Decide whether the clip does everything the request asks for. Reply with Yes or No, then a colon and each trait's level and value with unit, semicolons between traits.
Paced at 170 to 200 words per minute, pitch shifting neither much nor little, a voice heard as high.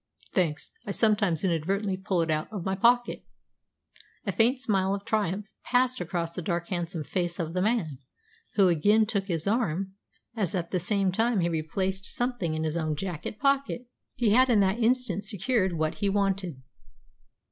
Yes: average, 175 wpm; average, 4.2 semitones; high, 195 Hz